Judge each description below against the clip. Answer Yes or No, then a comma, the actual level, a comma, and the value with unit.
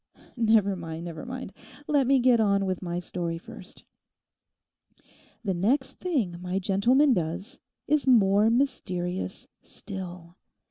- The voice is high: Yes, high, 195 Hz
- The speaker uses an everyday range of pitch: No, wide, 5.8 semitones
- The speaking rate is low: Yes, slow, 125 wpm